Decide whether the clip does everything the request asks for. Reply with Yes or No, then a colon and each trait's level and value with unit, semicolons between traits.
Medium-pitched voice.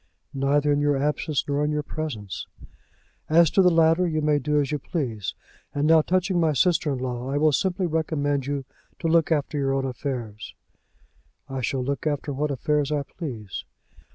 Yes: medium, 145 Hz